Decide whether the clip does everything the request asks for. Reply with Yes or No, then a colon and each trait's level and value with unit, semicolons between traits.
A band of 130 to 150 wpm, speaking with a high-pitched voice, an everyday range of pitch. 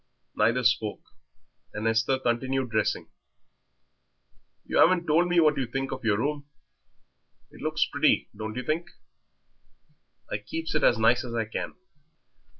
No: average, 145 wpm; low, 125 Hz; average, 5.0 semitones